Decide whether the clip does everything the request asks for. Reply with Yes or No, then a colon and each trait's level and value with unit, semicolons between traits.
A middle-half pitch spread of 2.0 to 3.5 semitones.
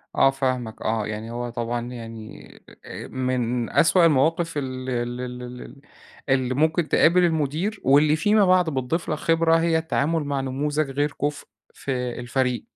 No: average, 4.6 semitones